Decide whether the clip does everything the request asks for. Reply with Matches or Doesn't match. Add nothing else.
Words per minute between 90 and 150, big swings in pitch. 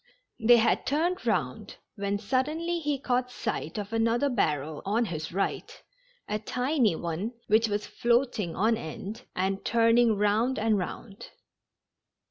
Doesn't match